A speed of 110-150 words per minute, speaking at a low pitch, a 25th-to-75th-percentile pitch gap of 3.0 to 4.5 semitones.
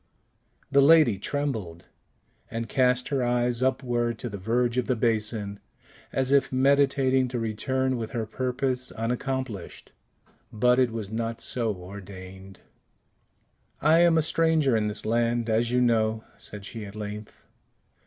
Yes: average, 145 wpm; low, 120 Hz; average, 3.3 semitones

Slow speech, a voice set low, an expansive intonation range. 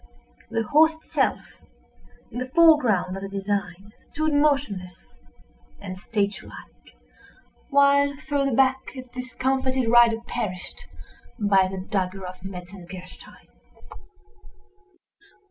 No: slow, 100 wpm; high, 215 Hz; wide, 6.2 semitones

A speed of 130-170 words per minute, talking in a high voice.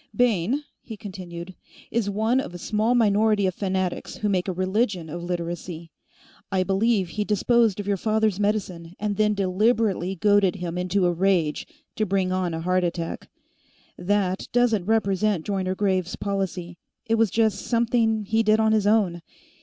Yes: average, 165 wpm; high, 195 Hz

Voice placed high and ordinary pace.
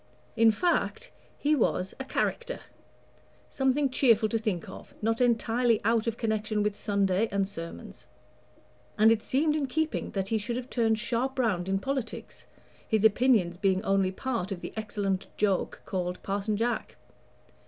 Yes: high, 220 Hz; average, 160 wpm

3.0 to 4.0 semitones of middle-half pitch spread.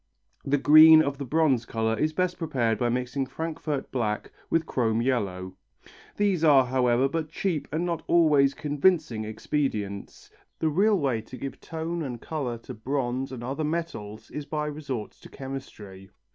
No: average, 4.8 semitones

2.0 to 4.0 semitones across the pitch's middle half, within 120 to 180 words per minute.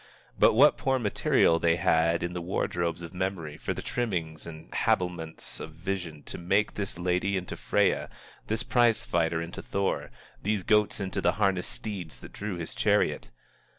Yes: average, 3.1 semitones; average, 170 wpm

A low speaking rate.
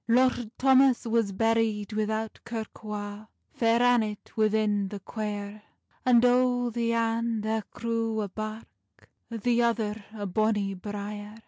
Yes: slow, 130 wpm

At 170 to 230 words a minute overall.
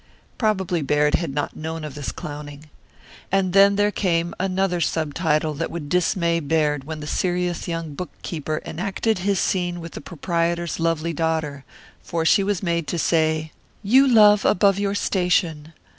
No: average, 155 wpm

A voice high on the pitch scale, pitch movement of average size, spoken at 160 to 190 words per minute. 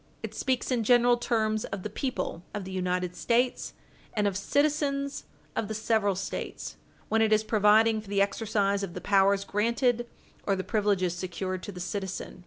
Yes: high, 210 Hz; average, 3.1 semitones; average, 180 wpm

